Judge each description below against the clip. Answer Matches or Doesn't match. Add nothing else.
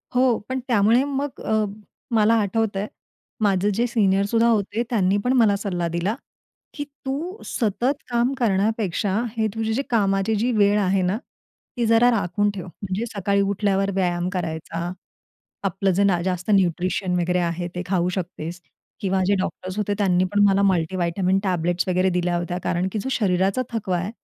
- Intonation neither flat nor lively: Matches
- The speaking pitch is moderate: Doesn't match